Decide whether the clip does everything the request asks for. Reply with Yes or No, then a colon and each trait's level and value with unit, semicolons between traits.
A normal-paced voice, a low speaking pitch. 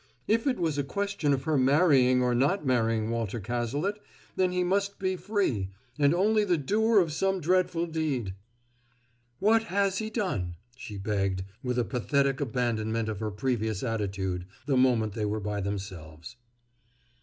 Yes: average, 160 wpm; low, 130 Hz